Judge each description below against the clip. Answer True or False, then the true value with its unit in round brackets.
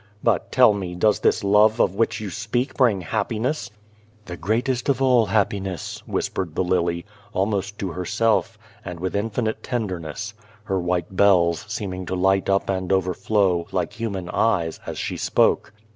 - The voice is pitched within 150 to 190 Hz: False (100 Hz)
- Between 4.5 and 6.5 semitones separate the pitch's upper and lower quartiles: False (3.4 semitones)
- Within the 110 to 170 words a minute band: True (160 wpm)